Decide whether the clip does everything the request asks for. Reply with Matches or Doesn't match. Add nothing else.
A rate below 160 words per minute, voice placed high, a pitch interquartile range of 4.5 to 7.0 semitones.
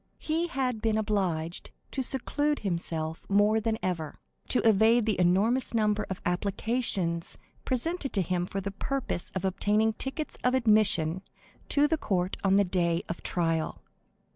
Matches